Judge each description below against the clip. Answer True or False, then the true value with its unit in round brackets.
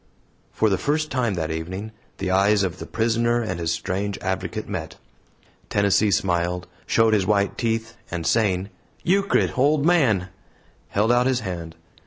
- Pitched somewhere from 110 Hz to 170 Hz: False (100 Hz)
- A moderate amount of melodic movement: True (4.2 semitones)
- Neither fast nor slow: True (155 wpm)